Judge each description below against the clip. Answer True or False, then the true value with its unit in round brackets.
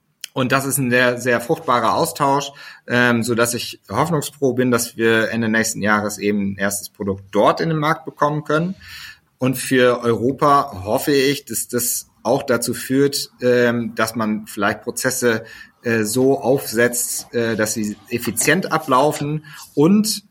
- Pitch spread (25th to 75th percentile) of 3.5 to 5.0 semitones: True (3.8 semitones)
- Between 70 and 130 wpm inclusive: False (155 wpm)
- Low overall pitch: True (125 Hz)